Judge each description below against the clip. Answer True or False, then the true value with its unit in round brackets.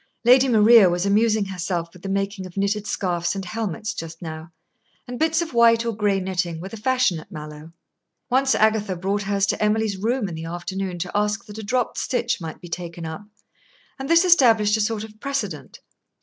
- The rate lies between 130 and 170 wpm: False (200 wpm)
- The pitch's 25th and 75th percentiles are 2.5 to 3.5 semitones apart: False (4.2 semitones)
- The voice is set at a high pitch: True (205 Hz)